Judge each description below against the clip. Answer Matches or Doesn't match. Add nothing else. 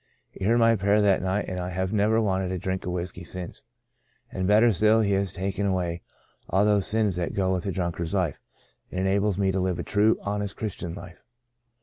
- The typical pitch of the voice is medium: Doesn't match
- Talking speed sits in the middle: Doesn't match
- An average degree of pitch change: Doesn't match